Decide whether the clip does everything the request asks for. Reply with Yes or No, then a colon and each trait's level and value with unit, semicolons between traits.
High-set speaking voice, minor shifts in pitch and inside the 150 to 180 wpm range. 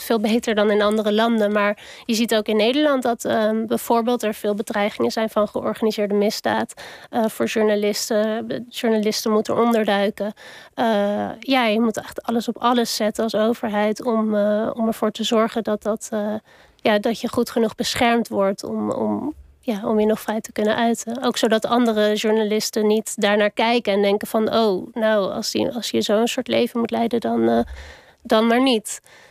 No: high, 220 Hz; narrow, 1.8 semitones; average, 190 wpm